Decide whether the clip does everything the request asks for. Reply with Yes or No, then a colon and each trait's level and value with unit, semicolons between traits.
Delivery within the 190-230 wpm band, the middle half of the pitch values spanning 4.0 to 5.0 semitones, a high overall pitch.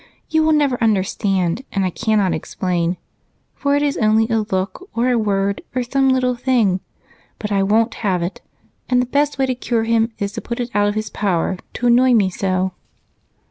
Yes: average, 200 wpm; average, 4.4 semitones; high, 220 Hz